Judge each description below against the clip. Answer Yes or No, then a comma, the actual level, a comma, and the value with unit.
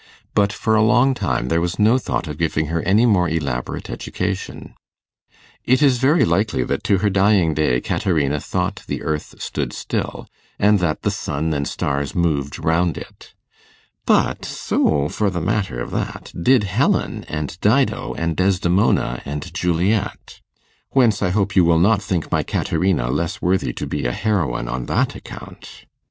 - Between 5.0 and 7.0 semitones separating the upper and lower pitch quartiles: Yes, wide, 5.5 semitones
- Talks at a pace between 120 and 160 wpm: No, average, 170 wpm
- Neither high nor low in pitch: No, very low, 85 Hz